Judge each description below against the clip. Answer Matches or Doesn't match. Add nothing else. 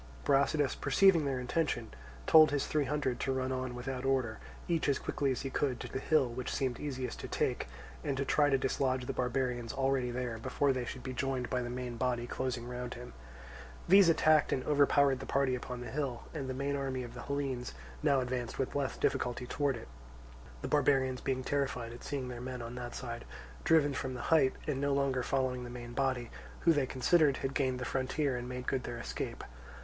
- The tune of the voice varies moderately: Doesn't match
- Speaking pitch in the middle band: Doesn't match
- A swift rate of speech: Matches